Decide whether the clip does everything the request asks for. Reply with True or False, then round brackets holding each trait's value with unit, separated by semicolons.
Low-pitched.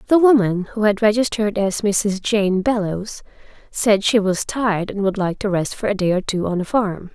False (205 Hz)